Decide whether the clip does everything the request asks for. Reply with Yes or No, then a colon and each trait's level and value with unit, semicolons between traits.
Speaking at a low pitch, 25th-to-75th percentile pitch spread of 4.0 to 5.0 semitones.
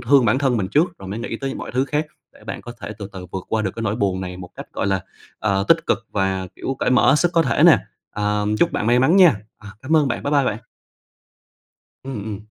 No: low, 115 Hz; wide, 5.4 semitones